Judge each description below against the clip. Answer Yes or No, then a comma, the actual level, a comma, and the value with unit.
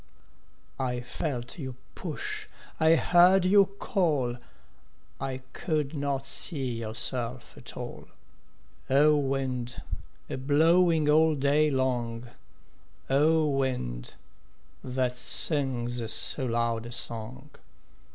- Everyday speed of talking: No, slow, 100 wpm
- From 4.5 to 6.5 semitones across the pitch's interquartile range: No, average, 3.8 semitones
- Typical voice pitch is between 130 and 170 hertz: Yes, low, 135 Hz